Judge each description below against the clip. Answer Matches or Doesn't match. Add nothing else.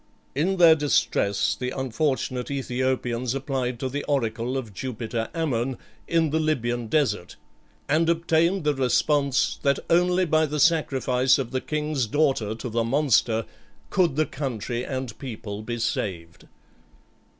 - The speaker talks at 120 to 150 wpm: Matches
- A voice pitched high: Doesn't match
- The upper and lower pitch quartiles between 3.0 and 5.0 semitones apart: Matches